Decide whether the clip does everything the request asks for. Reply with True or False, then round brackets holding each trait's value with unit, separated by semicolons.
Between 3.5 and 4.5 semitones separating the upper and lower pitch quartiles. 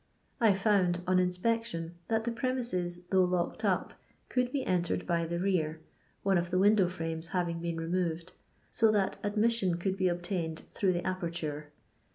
False (3.0 semitones)